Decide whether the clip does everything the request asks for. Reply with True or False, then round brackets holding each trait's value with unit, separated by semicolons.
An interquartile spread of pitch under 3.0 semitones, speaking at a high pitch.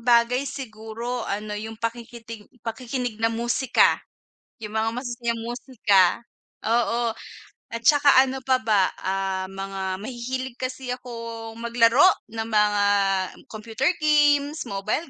True (2.5 semitones; 230 Hz)